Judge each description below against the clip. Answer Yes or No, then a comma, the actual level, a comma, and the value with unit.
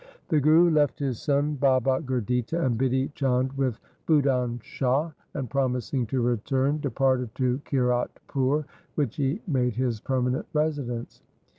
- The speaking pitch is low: Yes, low, 130 Hz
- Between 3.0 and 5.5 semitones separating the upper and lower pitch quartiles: No, narrow, 2.5 semitones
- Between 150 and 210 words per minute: No, slow, 135 wpm